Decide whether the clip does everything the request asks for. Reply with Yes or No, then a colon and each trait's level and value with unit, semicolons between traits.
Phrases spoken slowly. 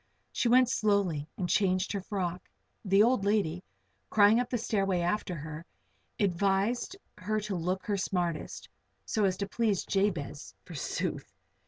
No: average, 145 wpm